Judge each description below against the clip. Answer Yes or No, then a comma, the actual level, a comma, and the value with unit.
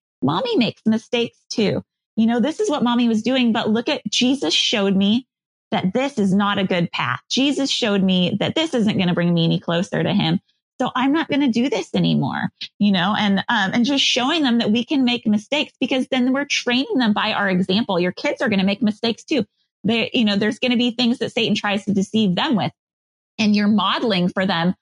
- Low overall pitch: No, high, 225 Hz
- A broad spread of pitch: No, average, 4.1 semitones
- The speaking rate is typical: No, fast, 230 wpm